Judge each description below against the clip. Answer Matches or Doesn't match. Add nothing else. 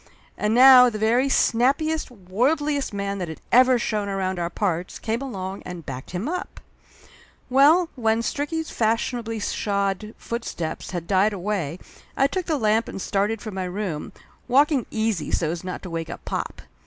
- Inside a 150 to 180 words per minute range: Matches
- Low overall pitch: Doesn't match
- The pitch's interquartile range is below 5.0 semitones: Doesn't match